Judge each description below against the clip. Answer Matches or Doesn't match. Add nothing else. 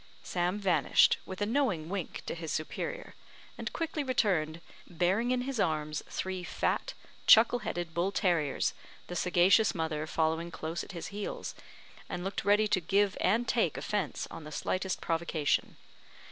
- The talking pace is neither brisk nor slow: Matches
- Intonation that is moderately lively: Matches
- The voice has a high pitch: Doesn't match